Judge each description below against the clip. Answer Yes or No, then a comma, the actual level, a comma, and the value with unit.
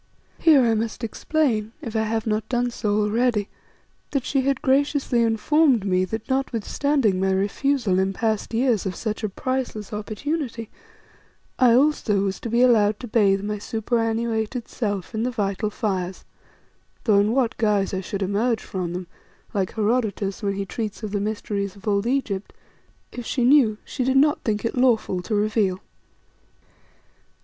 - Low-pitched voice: No, high, 220 Hz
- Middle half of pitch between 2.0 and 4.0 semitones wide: Yes, average, 3.4 semitones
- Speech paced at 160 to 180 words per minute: Yes, average, 165 wpm